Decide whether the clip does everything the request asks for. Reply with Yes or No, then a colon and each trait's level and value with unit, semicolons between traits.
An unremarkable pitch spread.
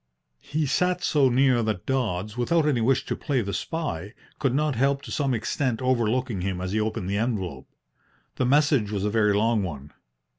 Yes: average, 4.9 semitones